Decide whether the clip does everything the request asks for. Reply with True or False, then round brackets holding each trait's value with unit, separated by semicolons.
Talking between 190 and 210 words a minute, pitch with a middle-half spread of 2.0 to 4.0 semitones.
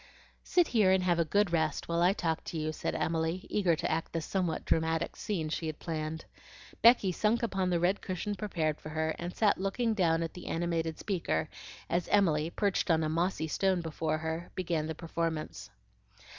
True (195 wpm; 2.9 semitones)